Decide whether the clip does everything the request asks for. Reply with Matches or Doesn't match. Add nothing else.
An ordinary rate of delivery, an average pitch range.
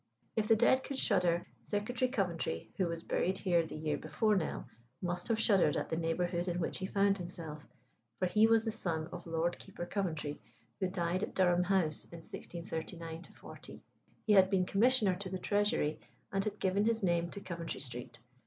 Matches